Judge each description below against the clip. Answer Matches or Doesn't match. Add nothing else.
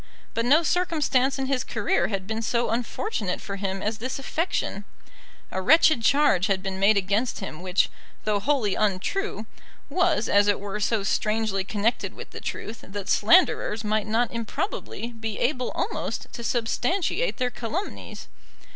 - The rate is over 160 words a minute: Doesn't match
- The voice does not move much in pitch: Doesn't match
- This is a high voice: Matches